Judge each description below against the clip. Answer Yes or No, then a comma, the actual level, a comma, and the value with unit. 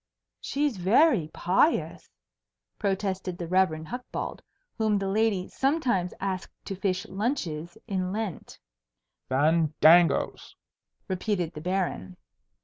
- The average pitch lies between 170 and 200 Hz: Yes, high, 190 Hz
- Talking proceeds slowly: Yes, slow, 100 wpm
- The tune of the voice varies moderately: Yes, average, 3.8 semitones